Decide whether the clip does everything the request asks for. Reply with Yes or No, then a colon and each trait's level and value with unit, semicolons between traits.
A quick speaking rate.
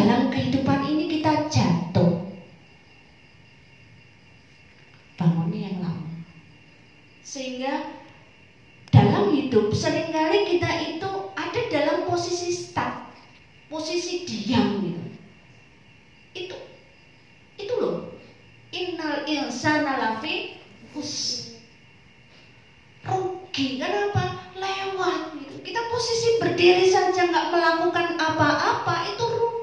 No: slow, 85 wpm